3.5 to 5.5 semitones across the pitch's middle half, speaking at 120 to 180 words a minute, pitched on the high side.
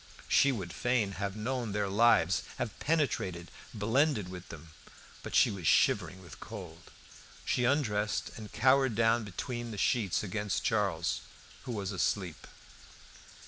No: average, 4.3 semitones; average, 140 wpm; low, 105 Hz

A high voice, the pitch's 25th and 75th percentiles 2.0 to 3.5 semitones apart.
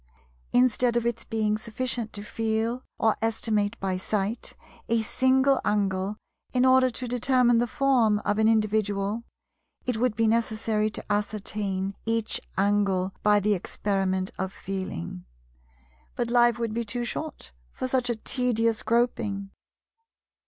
Yes: high, 220 Hz; narrow, 2.6 semitones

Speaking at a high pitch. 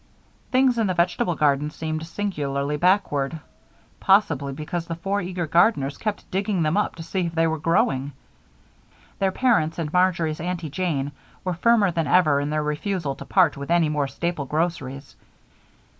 No: medium, 165 Hz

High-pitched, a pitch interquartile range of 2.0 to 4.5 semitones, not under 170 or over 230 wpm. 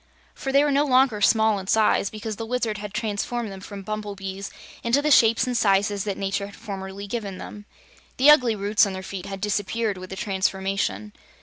Yes: high, 205 Hz; average, 2.8 semitones; average, 200 wpm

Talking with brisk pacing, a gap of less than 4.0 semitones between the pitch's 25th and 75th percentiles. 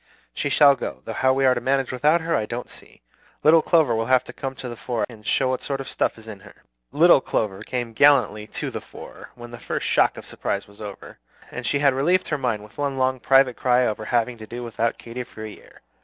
Yes: fast, 255 wpm; average, 3.2 semitones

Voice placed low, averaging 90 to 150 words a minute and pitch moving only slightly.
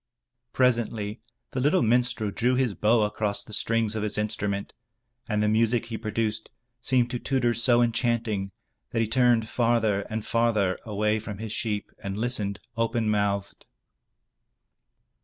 Yes: low, 110 Hz; average, 145 wpm; narrow, 2.2 semitones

